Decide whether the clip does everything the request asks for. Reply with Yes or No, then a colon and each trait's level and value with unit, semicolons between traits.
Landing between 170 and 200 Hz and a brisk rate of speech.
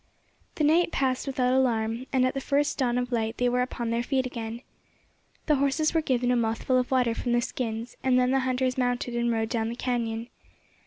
No: very high, 250 Hz; fast, 215 wpm